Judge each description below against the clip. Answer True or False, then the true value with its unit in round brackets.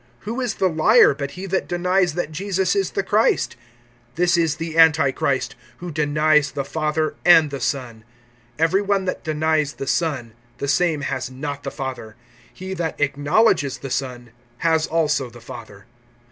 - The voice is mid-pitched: True (155 Hz)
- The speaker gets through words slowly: False (165 wpm)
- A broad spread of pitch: False (4.1 semitones)